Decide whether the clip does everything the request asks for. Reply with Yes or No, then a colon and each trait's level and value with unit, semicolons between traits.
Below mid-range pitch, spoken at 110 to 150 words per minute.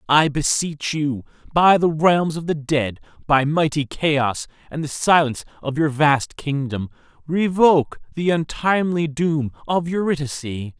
No: medium, 150 Hz; average, 140 wpm